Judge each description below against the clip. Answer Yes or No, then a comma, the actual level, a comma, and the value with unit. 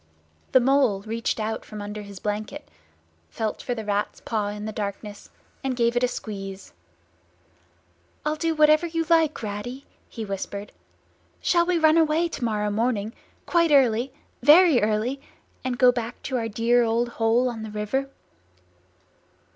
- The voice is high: Yes, high, 235 Hz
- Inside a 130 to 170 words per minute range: Yes, average, 150 wpm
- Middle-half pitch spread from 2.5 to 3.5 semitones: No, average, 4.6 semitones